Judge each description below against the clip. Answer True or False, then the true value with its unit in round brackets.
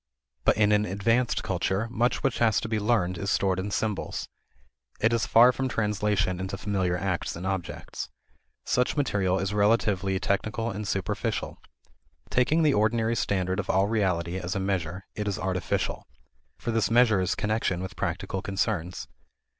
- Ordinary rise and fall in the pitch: True (3.0 semitones)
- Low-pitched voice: True (100 Hz)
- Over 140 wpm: True (160 wpm)